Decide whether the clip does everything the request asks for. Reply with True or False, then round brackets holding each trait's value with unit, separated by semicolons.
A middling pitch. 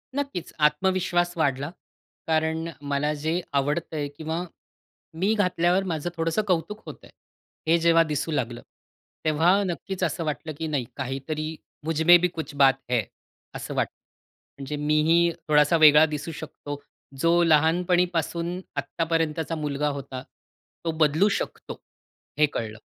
True (160 Hz)